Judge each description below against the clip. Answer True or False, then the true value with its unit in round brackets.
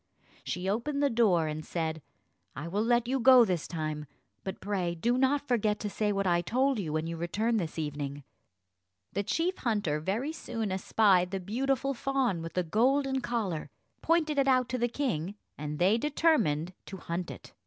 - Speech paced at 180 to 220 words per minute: True (185 wpm)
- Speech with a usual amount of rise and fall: False (7.0 semitones)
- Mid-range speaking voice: False (205 Hz)